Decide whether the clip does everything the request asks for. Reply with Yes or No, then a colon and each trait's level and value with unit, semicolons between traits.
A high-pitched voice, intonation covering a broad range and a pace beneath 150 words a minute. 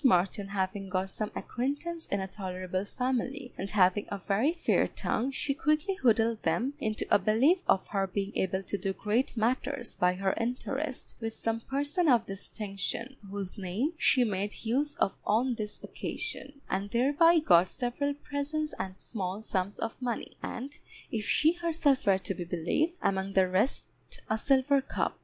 No: high, 225 Hz; wide, 6.1 semitones; average, 170 wpm